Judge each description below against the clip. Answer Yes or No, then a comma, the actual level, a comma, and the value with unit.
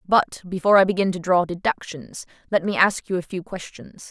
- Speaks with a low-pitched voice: No, medium, 185 Hz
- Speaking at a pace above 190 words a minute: Yes, fast, 205 wpm